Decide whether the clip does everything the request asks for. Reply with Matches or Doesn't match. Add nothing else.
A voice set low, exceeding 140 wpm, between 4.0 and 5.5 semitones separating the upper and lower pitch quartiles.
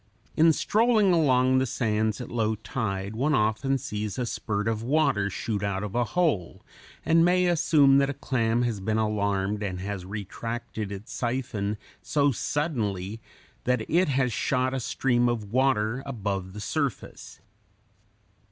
Matches